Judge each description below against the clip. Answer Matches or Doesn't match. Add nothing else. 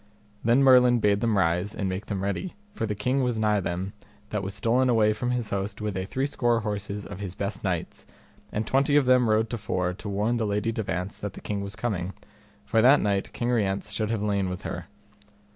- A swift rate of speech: Matches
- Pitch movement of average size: Matches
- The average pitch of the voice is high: Doesn't match